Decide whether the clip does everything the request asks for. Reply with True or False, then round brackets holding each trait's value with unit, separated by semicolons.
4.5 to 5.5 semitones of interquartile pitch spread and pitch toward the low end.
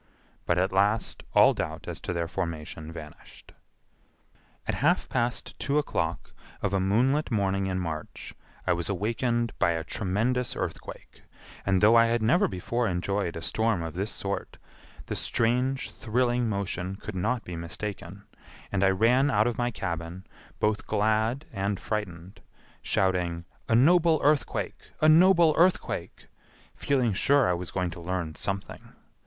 True (5.0 semitones; 100 Hz)